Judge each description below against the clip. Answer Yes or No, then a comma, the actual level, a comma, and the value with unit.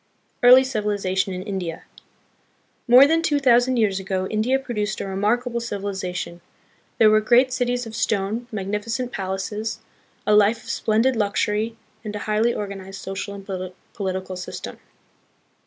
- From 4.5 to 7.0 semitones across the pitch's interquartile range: No, average, 3.6 semitones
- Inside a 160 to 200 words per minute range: No, average, 145 wpm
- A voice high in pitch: Yes, high, 215 Hz